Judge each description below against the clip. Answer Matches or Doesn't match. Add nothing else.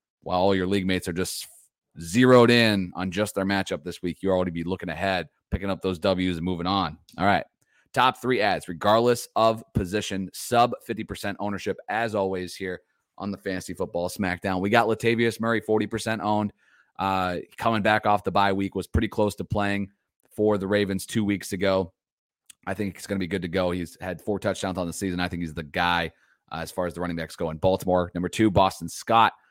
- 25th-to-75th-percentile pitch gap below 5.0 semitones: Matches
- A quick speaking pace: Matches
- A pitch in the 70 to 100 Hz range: Matches